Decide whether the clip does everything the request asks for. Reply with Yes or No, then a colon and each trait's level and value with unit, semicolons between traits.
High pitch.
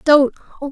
Yes: very high, 280 Hz